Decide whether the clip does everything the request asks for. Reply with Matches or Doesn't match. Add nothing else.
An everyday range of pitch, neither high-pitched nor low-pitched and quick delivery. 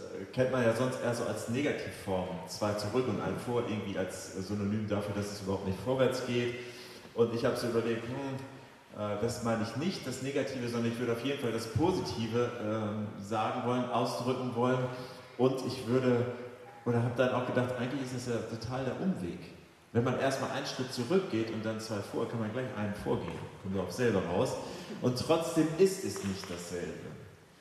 Doesn't match